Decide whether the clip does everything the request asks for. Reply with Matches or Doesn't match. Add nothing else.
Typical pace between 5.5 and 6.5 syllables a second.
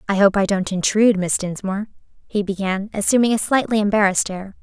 Matches